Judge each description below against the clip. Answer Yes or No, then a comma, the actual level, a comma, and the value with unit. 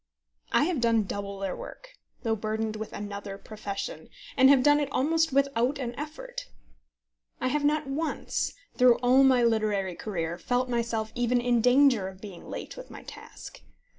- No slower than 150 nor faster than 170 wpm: Yes, average, 165 wpm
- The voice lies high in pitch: Yes, high, 240 Hz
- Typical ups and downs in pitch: Yes, average, 4.6 semitones